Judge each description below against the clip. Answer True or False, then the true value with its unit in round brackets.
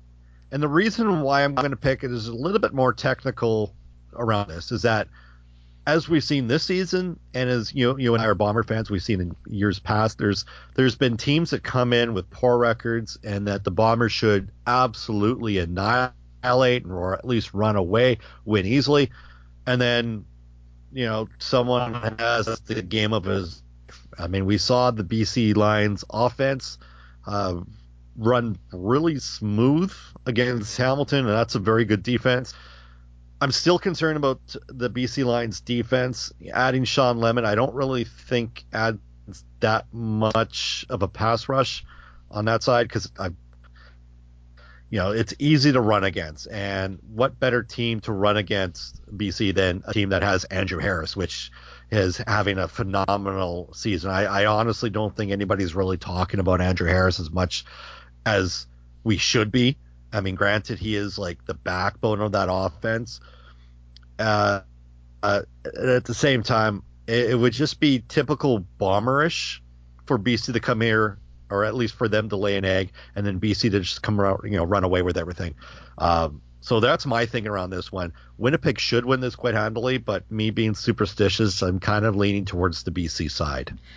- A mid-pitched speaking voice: False (105 Hz)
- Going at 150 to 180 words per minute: True (170 wpm)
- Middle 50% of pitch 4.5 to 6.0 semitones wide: True (5.0 semitones)